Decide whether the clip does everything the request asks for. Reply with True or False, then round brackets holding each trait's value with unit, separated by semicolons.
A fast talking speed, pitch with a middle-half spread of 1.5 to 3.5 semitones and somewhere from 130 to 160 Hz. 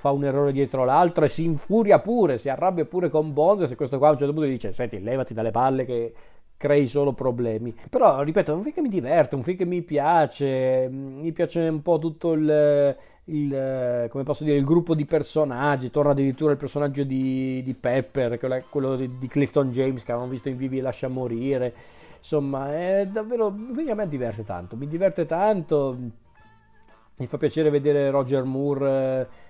True (185 wpm; 3.0 semitones; 140 Hz)